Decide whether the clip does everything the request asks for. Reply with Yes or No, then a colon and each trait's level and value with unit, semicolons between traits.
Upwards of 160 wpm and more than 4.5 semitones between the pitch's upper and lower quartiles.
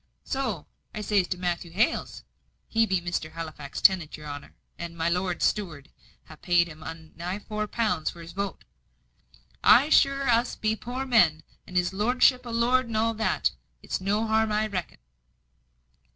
Yes: average, 170 wpm; average, 4.9 semitones